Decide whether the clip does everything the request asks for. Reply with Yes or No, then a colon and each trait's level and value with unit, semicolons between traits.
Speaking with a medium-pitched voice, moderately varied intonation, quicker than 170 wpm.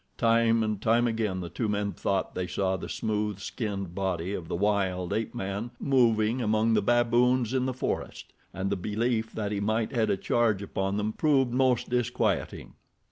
No: low, 110 Hz; average, 3.2 semitones; average, 185 wpm